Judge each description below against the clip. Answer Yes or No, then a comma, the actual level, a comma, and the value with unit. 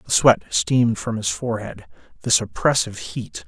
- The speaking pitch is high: No, low, 115 Hz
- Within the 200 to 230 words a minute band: No, average, 155 wpm